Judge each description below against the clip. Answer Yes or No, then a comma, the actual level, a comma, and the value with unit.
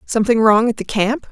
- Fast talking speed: Yes, fast, 225 wpm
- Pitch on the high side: Yes, high, 225 Hz